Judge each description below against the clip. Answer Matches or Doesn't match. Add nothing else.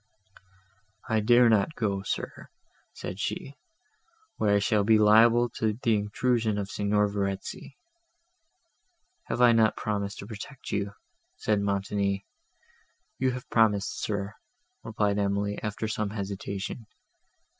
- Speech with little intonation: Matches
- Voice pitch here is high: Doesn't match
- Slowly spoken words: Matches